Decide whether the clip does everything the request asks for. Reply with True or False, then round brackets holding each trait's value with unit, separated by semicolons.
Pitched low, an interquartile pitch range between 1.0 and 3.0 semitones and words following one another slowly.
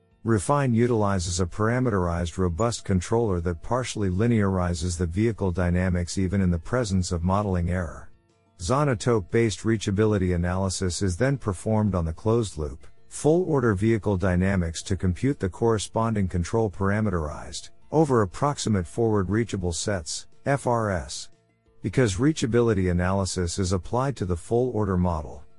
False (100 Hz; 4.0 semitones; 120 wpm)